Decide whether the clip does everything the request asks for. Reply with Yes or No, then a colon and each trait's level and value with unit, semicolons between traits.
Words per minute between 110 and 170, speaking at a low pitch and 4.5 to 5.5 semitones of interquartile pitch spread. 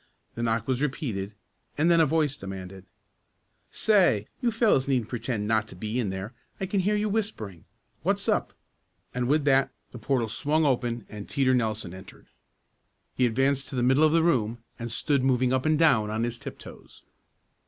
No: average, 185 wpm; low, 125 Hz; average, 5.2 semitones